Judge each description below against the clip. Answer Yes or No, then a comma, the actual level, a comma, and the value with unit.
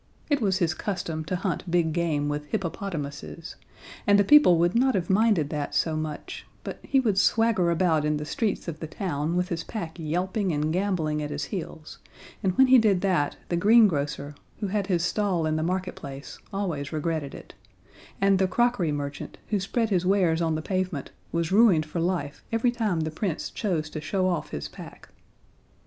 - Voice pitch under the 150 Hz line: No, medium, 175 Hz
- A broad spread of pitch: No, average, 4.1 semitones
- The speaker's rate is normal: Yes, average, 190 wpm